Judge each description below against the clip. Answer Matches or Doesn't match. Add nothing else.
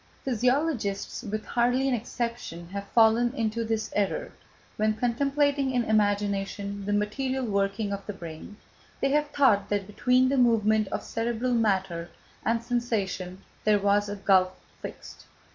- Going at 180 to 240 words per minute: Doesn't match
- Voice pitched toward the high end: Matches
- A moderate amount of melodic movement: Matches